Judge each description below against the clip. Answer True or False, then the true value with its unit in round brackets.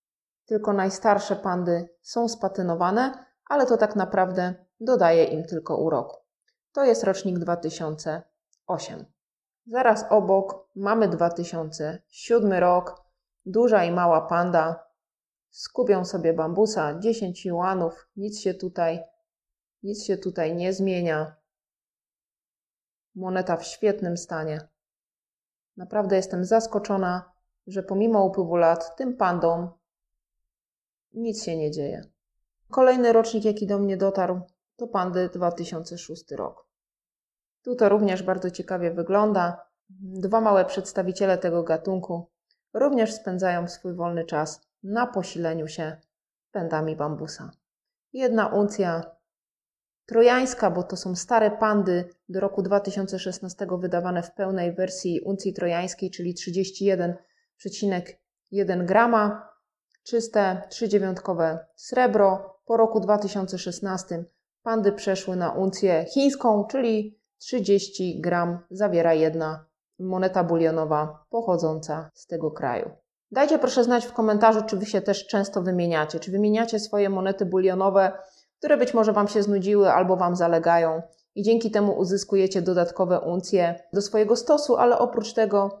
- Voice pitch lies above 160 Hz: True (190 Hz)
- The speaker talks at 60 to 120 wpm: True (115 wpm)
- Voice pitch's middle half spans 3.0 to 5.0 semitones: True (3.5 semitones)